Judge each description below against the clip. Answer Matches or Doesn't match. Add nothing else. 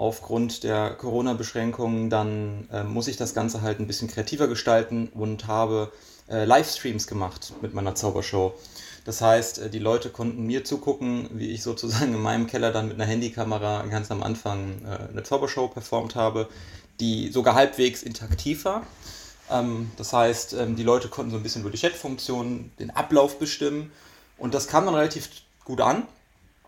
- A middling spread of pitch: Doesn't match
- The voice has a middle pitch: Doesn't match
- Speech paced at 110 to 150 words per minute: Doesn't match